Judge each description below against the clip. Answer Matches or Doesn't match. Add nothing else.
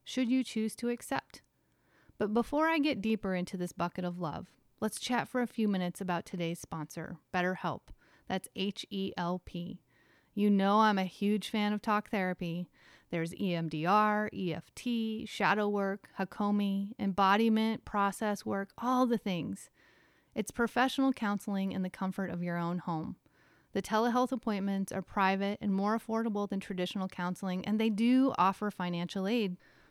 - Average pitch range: Matches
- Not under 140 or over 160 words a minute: Matches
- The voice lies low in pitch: Doesn't match